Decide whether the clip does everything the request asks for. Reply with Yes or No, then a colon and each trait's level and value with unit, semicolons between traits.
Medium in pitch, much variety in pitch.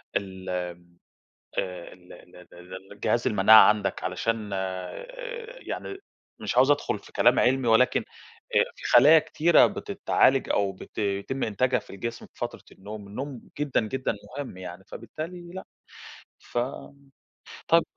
No: low, 110 Hz; wide, 6.5 semitones